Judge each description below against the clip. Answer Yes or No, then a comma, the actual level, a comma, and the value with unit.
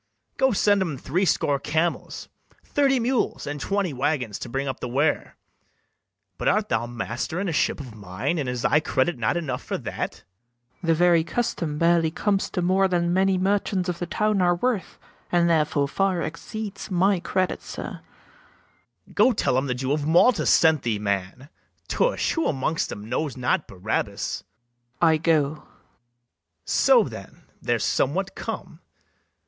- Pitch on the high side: No, medium, 165 Hz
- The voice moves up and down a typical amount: No, wide, 6.0 semitones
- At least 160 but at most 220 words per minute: Yes, average, 165 wpm